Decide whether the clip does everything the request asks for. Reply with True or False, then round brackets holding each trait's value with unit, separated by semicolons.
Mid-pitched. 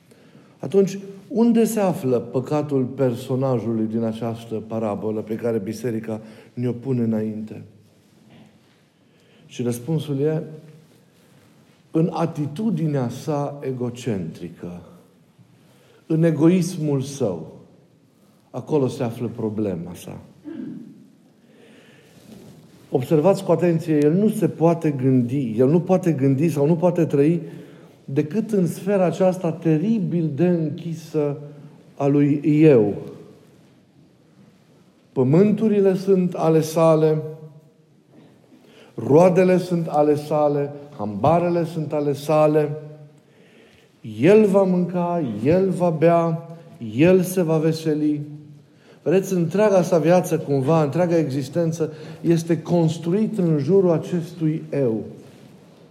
True (155 Hz)